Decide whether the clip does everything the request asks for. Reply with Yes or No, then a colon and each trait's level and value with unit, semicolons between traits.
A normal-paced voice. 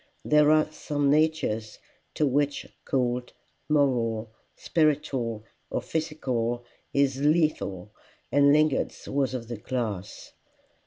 No: slow, 105 wpm